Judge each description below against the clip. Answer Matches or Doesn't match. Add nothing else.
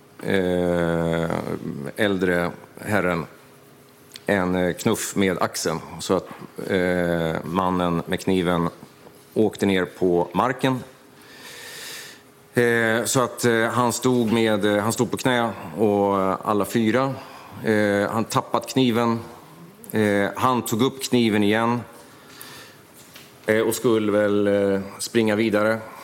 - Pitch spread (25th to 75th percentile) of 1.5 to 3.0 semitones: Doesn't match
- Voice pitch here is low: Matches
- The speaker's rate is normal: Doesn't match